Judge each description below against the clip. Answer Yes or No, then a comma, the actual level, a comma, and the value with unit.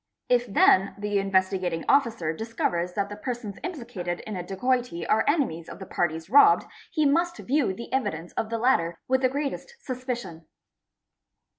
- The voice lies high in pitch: Yes, high, 220 Hz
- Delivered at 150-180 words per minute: Yes, average, 160 wpm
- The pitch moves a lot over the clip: Yes, wide, 6.3 semitones